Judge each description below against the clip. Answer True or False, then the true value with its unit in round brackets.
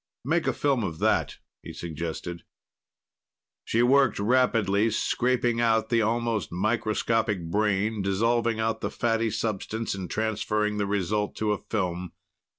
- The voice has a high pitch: False (110 Hz)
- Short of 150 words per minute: True (135 wpm)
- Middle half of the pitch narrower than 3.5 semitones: True (2.7 semitones)